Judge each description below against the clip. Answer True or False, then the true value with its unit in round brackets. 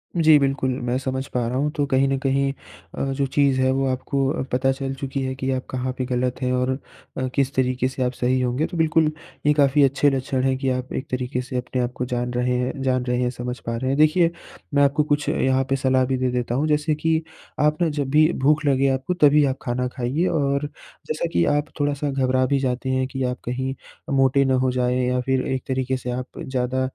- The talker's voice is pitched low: True (130 Hz)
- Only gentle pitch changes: True (1.8 semitones)